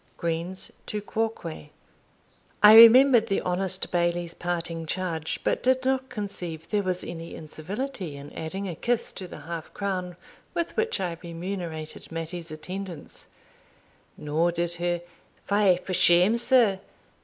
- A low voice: No, medium, 180 Hz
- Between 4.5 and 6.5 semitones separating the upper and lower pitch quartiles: No, average, 3.8 semitones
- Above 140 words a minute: No, slow, 135 wpm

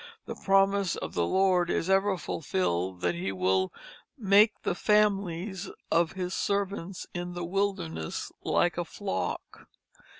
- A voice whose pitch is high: No, medium, 180 Hz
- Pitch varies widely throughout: No, average, 3.4 semitones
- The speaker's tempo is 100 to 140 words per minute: Yes, slow, 135 wpm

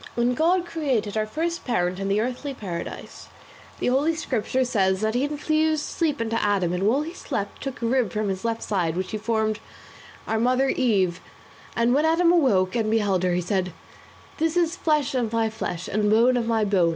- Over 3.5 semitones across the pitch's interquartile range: Yes, wide, 5.6 semitones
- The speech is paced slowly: No, fast, 205 wpm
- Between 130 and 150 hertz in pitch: No, high, 230 Hz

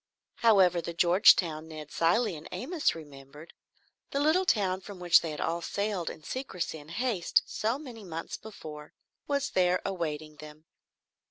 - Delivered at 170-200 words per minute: No, average, 155 wpm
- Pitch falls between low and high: Yes, medium, 175 Hz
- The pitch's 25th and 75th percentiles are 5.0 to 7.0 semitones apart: Yes, wide, 5.5 semitones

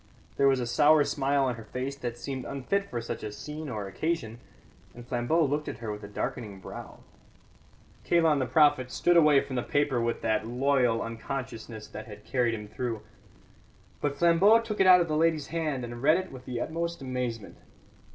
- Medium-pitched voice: No, low, 130 Hz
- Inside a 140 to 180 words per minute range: No, average, 195 wpm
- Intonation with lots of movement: No, average, 4.6 semitones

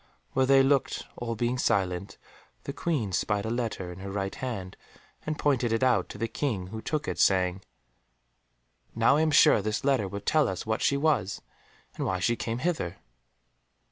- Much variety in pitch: Yes, wide, 5.7 semitones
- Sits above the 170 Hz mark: No, low, 115 Hz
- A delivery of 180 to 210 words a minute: Yes, average, 185 wpm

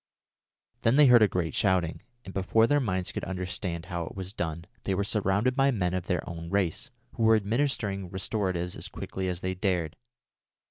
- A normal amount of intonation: Yes, average, 3.3 semitones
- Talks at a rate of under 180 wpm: No, average, 190 wpm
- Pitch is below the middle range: Yes, very low, 95 Hz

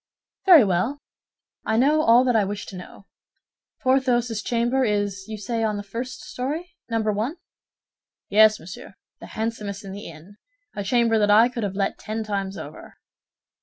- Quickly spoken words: No, average, 165 wpm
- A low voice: No, high, 220 Hz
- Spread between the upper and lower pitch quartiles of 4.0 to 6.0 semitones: No, average, 3.4 semitones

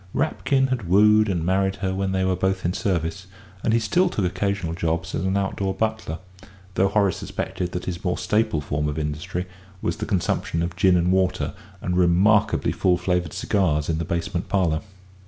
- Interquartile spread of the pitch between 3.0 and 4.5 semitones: No, narrow, 2.6 semitones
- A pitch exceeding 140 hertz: No, very low, 95 Hz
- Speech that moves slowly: No, average, 190 wpm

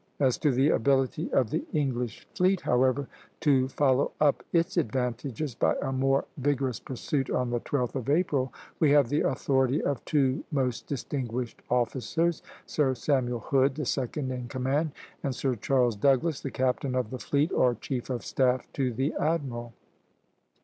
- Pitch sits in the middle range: No, low, 130 Hz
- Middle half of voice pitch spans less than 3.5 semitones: Yes, narrow, 2.4 semitones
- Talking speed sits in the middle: Yes, average, 165 wpm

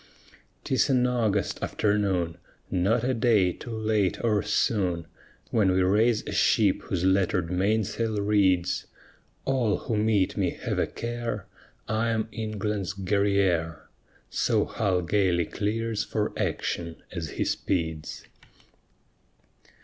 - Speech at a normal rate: No, slow, 120 wpm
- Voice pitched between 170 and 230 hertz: No, low, 105 Hz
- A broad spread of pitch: No, average, 3.1 semitones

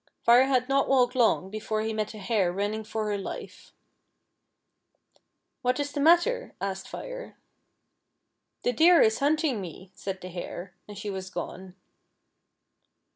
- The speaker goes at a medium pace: Yes, average, 165 wpm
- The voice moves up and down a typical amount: No, wide, 5.9 semitones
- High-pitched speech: Yes, high, 220 Hz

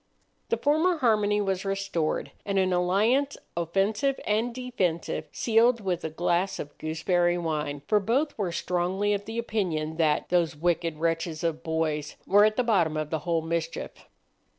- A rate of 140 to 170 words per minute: Yes, average, 160 wpm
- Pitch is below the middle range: No, medium, 180 Hz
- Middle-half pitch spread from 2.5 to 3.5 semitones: No, average, 4.7 semitones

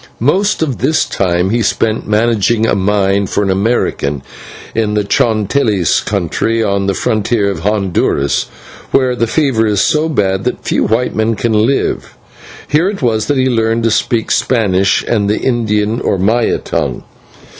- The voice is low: Yes, low, 110 Hz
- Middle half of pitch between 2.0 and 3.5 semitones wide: Yes, average, 3.1 semitones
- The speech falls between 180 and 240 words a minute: No, average, 165 wpm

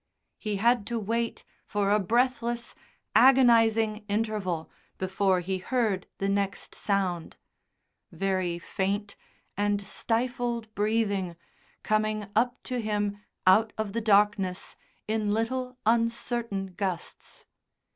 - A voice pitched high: Yes, high, 210 Hz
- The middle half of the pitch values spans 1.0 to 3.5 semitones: Yes, average, 2.8 semitones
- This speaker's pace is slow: Yes, slow, 105 wpm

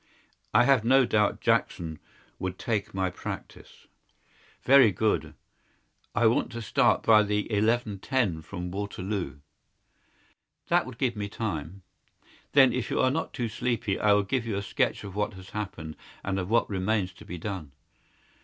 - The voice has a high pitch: No, low, 105 Hz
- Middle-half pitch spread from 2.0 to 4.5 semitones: Yes, average, 3.7 semitones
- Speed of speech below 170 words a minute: Yes, average, 160 wpm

